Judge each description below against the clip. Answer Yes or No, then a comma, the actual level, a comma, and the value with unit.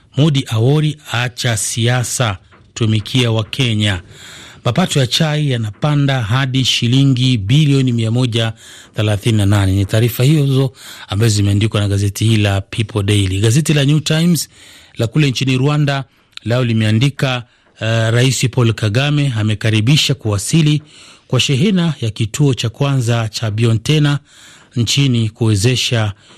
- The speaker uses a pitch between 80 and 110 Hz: No, low, 120 Hz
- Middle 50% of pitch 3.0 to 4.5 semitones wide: Yes, average, 4.0 semitones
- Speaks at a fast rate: No, average, 120 wpm